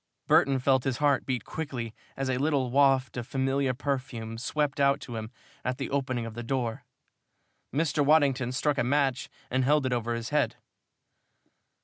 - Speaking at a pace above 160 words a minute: Yes, average, 170 wpm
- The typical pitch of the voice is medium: No, low, 130 Hz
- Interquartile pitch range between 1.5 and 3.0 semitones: Yes, narrow, 2.5 semitones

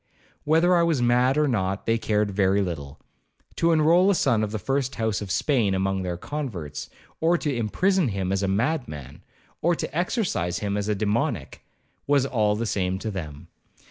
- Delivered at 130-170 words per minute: No, average, 185 wpm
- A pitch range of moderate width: No, wide, 7.2 semitones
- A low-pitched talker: Yes, low, 110 Hz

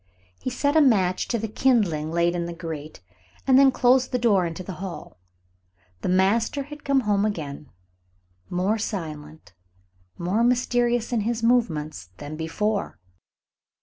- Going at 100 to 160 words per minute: Yes, average, 150 wpm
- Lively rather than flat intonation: Yes, wide, 6.3 semitones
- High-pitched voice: Yes, high, 205 Hz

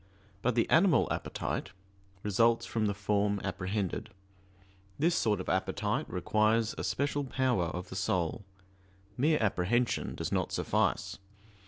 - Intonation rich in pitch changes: No, average, 4.3 semitones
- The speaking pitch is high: No, low, 110 Hz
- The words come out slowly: Yes, slow, 130 wpm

